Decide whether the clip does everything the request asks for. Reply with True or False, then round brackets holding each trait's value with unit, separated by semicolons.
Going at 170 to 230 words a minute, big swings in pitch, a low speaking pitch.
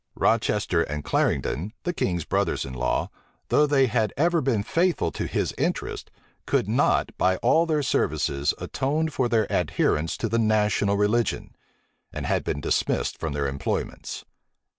False (155 wpm; 8.5 semitones; 110 Hz)